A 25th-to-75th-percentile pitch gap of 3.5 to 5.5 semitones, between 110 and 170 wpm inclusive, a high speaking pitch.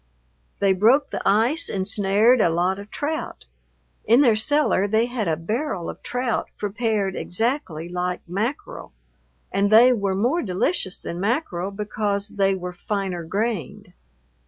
Yes: average, 4.0 semitones; average, 145 wpm; high, 205 Hz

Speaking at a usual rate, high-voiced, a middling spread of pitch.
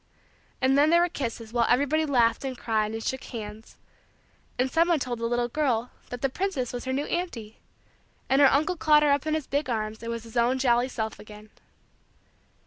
No: fast, 210 wpm; very high, 255 Hz; average, 3.9 semitones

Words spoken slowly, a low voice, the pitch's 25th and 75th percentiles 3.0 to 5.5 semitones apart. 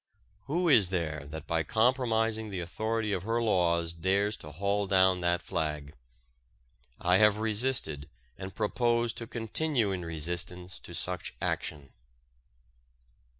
Yes: slow, 130 wpm; very low, 95 Hz; average, 4.8 semitones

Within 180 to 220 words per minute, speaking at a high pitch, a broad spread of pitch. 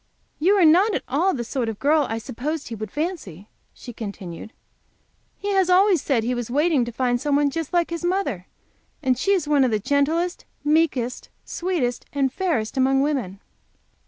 Yes: average, 190 wpm; very high, 280 Hz; wide, 5.9 semitones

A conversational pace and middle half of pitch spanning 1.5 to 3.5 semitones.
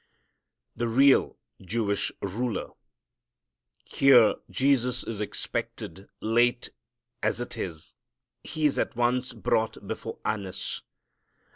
No: slow, 100 wpm; average, 3.0 semitones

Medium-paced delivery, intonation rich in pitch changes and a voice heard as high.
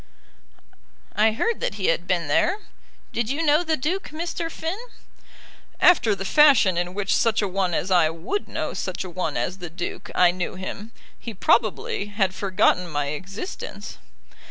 Yes: average, 170 wpm; wide, 8.0 semitones; high, 200 Hz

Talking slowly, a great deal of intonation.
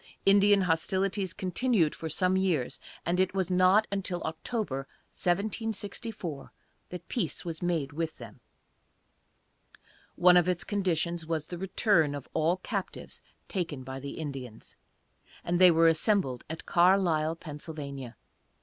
No: slow, 130 wpm; average, 3.3 semitones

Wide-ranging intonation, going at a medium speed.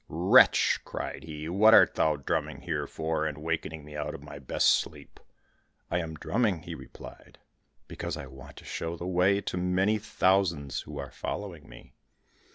No: average, 3.6 semitones; average, 170 wpm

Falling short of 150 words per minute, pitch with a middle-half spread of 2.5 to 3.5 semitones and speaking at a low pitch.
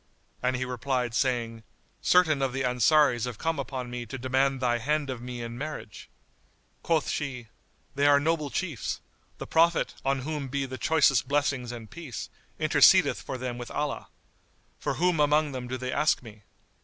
No: average, 175 wpm; average, 3.2 semitones; low, 130 Hz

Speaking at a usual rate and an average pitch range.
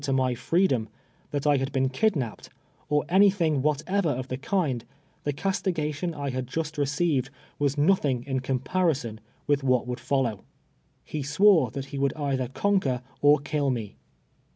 Yes: average, 160 wpm; average, 3.4 semitones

